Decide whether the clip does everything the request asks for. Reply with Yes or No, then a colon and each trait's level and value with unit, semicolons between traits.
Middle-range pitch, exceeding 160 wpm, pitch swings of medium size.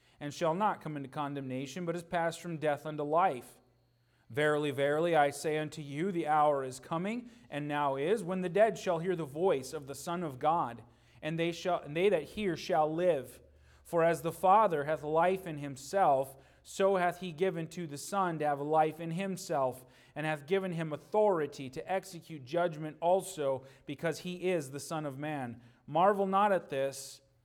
Yes: medium, 155 Hz; average, 190 wpm; average, 4.0 semitones